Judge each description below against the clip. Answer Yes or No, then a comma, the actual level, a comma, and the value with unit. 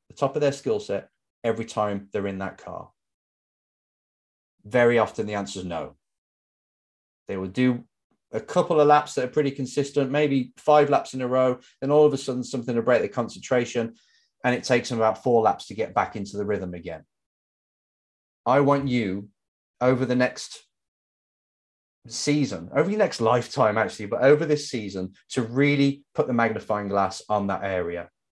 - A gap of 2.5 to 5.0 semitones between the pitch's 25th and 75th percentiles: No, wide, 5.6 semitones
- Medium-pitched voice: No, low, 120 Hz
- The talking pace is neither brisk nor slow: Yes, average, 180 wpm